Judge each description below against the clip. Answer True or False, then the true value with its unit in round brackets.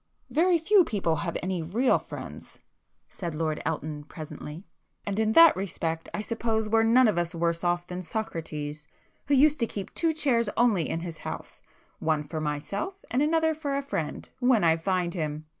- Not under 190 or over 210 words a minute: False (175 wpm)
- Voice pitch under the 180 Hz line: False (190 Hz)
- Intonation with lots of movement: True (7.7 semitones)